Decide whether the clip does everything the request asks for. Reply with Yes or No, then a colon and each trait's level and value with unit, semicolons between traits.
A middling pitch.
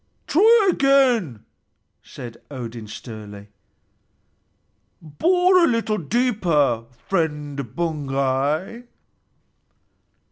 Yes: medium, 155 Hz